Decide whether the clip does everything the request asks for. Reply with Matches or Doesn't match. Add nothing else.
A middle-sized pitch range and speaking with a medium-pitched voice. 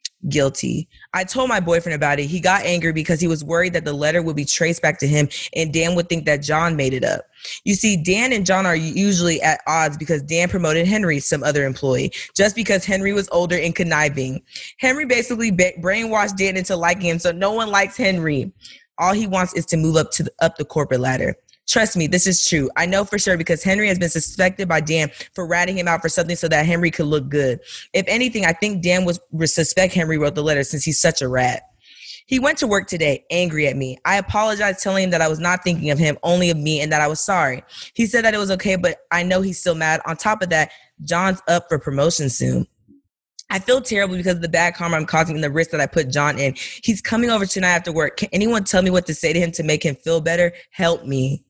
Matches